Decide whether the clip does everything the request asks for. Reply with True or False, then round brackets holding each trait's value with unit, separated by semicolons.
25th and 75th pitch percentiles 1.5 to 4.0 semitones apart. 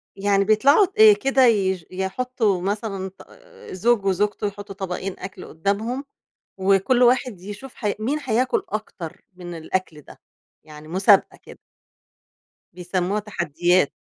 True (3.2 semitones)